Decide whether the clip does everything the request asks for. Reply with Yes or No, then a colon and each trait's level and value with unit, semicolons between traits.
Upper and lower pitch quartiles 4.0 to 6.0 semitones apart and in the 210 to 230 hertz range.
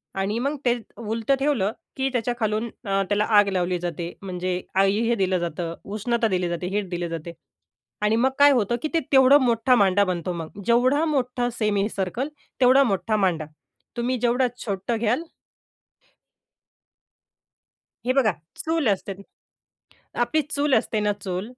Yes: average, 4.7 semitones; high, 215 Hz